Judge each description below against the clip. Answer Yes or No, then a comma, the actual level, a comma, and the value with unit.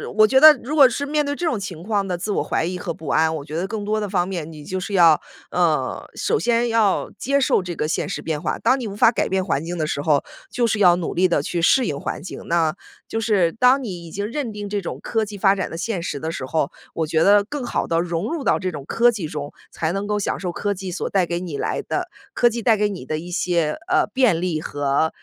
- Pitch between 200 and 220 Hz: No, high, 190 Hz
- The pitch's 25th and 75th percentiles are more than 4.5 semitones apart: Yes, average, 5.2 semitones